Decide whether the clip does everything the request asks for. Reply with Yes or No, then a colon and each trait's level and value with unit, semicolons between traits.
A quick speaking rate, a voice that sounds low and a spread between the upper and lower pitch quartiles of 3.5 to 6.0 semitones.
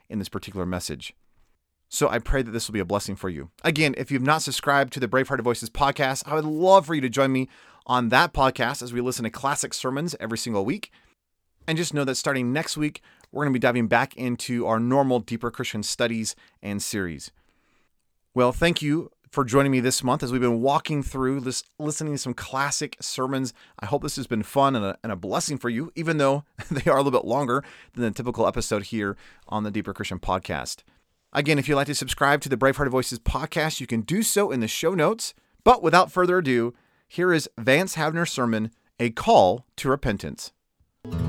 Yes: fast, 215 wpm; low, 130 Hz; average, 3.9 semitones